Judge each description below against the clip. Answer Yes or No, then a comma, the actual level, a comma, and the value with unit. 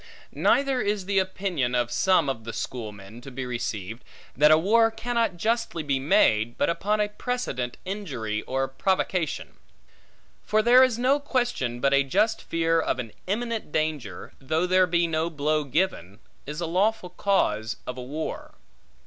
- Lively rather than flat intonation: Yes, wide, 8.5 semitones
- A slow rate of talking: No, average, 165 wpm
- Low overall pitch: No, medium, 165 Hz